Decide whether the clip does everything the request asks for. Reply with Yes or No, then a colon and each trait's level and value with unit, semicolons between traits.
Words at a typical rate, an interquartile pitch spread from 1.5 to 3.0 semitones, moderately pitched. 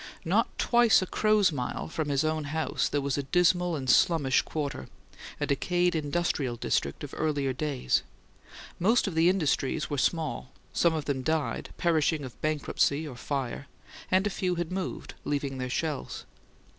No: average, 165 wpm; average, 3.8 semitones; medium, 155 Hz